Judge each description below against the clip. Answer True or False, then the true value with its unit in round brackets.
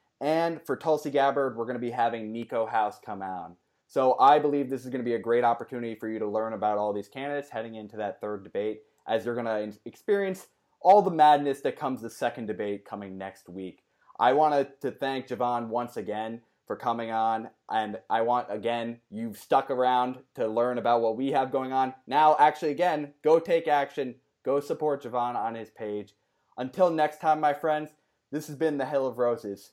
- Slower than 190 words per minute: False (205 wpm)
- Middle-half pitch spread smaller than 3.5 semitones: False (4.7 semitones)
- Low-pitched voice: True (125 Hz)